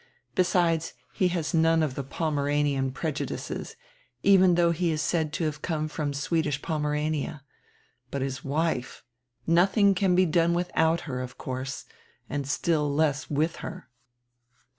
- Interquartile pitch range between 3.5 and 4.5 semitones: No, average, 2.9 semitones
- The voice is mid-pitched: Yes, medium, 155 Hz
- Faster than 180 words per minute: No, average, 145 wpm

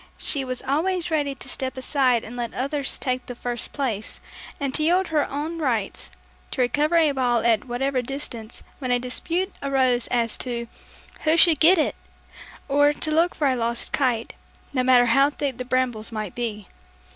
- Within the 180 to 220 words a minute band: Yes, average, 185 wpm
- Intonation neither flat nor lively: Yes, average, 3.4 semitones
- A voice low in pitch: No, very high, 260 Hz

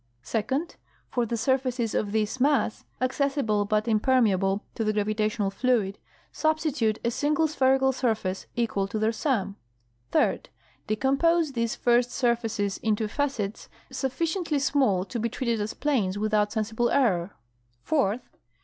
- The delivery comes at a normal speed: No, slow, 130 wpm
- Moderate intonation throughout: Yes, average, 4.0 semitones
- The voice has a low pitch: No, high, 230 Hz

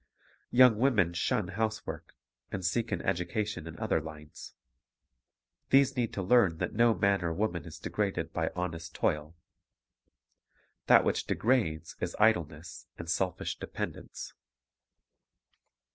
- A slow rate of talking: Yes, slow, 125 wpm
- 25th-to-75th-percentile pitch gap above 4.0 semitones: Yes, average, 5.1 semitones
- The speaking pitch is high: No, very low, 90 Hz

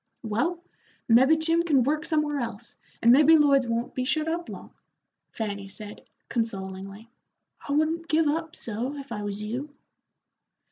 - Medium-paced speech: Yes, average, 150 wpm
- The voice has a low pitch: No, very high, 265 Hz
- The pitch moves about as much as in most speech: No, wide, 5.8 semitones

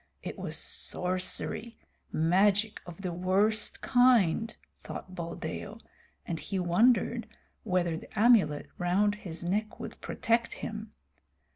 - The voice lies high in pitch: Yes, high, 195 Hz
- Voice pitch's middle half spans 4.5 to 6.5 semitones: No, average, 3.9 semitones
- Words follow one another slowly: Yes, slow, 115 wpm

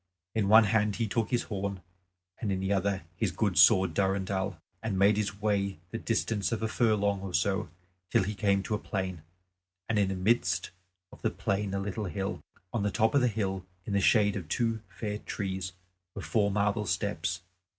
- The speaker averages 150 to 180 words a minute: No, average, 200 wpm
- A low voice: Yes, low, 100 Hz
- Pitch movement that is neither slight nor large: No, narrow, 2.0 semitones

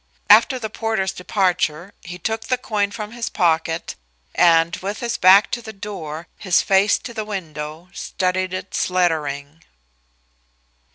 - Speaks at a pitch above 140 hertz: Yes, medium, 185 Hz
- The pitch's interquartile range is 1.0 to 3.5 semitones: No, average, 4.1 semitones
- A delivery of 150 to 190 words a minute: No, average, 140 wpm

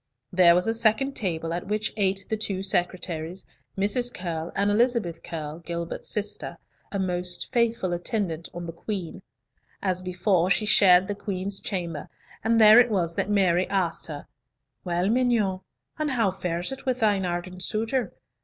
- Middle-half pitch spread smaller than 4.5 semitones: Yes, average, 3.6 semitones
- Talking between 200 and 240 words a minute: No, average, 165 wpm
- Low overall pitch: No, high, 190 Hz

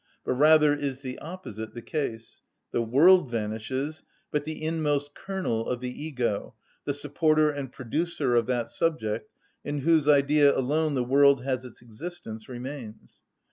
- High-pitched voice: No, medium, 140 Hz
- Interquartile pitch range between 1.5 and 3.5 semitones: No, average, 4.1 semitones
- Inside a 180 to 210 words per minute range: No, average, 150 wpm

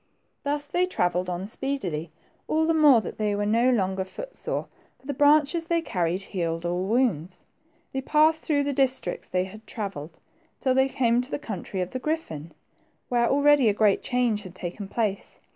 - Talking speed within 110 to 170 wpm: No, average, 185 wpm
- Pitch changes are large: Yes, wide, 7.3 semitones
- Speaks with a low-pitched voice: No, high, 230 Hz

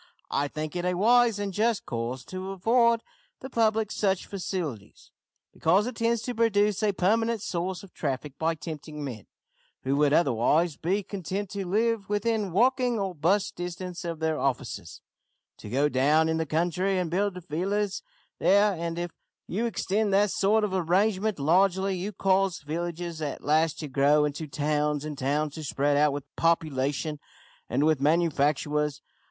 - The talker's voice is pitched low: No, medium, 175 Hz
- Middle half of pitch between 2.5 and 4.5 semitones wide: No, average, 5.2 semitones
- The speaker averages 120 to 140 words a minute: No, average, 165 wpm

